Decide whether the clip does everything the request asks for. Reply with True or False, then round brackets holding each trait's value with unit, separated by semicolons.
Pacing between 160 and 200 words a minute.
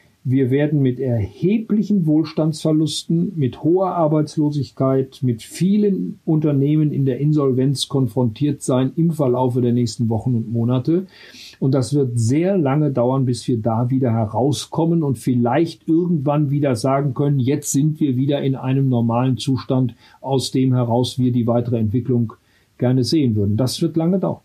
False (150 wpm)